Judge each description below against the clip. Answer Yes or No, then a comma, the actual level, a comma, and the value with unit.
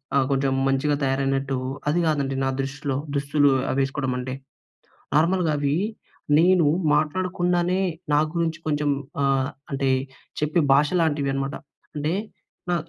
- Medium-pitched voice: Yes, medium, 145 Hz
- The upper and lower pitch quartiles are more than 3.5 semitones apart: No, average, 2.7 semitones